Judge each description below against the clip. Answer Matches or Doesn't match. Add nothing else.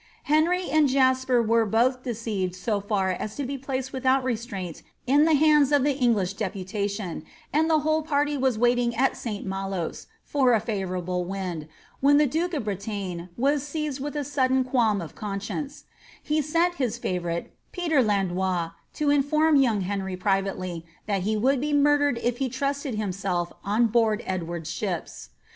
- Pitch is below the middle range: Doesn't match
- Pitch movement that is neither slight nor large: Doesn't match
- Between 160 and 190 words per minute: Matches